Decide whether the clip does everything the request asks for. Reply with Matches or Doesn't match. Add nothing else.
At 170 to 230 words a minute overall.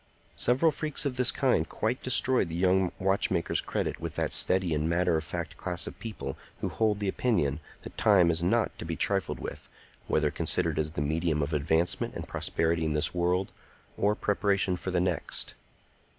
Matches